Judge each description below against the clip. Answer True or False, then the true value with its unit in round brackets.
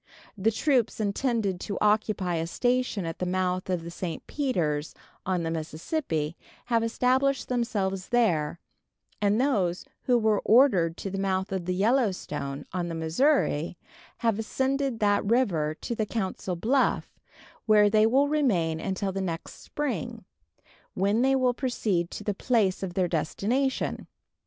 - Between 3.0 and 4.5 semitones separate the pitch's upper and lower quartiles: False (5.5 semitones)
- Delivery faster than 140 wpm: True (150 wpm)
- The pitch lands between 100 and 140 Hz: False (200 Hz)